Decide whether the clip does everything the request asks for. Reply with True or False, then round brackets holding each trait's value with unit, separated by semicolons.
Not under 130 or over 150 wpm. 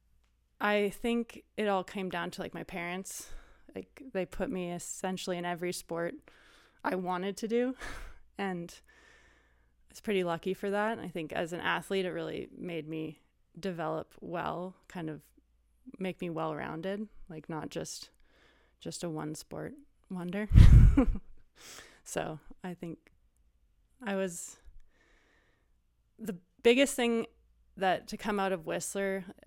True (140 wpm)